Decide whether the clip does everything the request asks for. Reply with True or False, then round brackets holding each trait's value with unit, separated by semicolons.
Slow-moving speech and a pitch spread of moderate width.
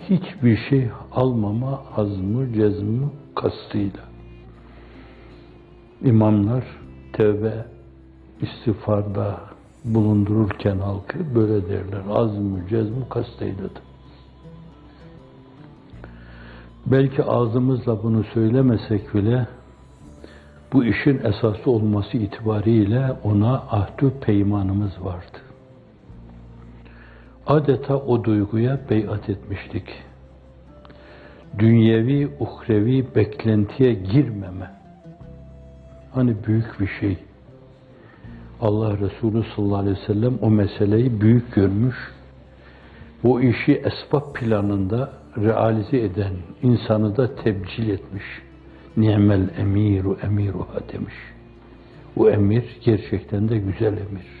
True (80 wpm; 3.5 semitones)